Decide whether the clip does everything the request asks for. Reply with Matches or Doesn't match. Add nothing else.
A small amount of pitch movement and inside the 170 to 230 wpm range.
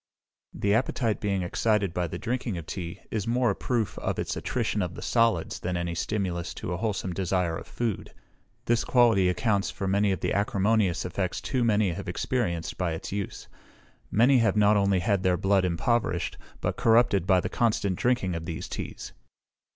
Doesn't match